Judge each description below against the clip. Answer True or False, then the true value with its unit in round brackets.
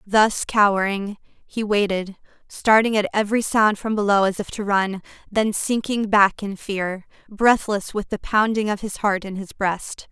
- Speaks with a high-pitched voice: True (205 Hz)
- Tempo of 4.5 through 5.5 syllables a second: False (4.3 syllables/s)